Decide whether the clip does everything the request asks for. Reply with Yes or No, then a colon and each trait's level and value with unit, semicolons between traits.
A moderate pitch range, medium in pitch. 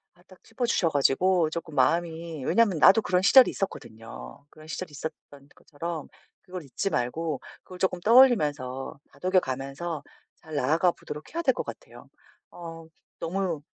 Yes: average, 4.2 semitones; medium, 165 Hz